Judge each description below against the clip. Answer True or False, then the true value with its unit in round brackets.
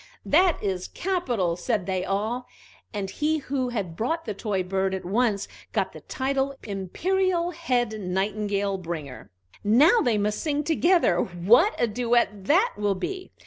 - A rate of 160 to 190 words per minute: False (150 wpm)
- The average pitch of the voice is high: True (220 Hz)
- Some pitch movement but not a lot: False (7.4 semitones)